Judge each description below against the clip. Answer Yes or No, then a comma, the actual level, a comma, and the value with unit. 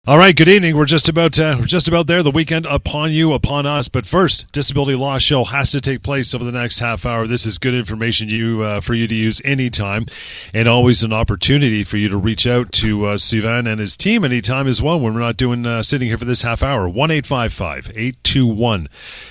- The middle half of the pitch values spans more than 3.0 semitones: Yes, average, 4.2 semitones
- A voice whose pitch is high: No, low, 125 Hz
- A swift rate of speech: Yes, fast, 225 wpm